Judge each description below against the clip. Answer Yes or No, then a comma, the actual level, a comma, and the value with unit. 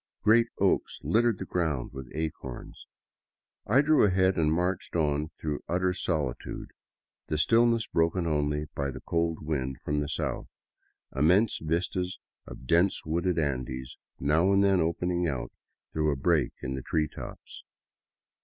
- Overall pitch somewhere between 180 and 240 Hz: No, very low, 80 Hz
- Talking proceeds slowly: No, average, 150 wpm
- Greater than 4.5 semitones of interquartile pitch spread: No, average, 3.8 semitones